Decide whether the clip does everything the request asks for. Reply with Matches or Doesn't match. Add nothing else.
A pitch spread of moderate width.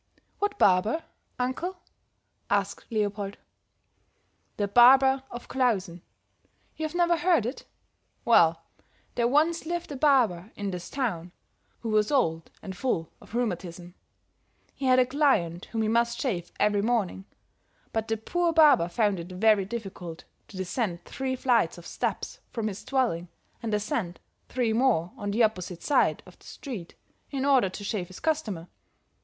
Doesn't match